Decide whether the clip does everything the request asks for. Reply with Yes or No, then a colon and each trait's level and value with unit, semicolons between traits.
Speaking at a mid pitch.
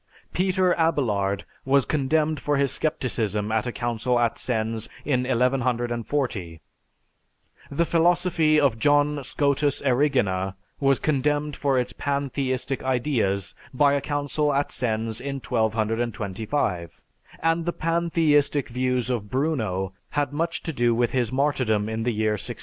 No: low, 130 Hz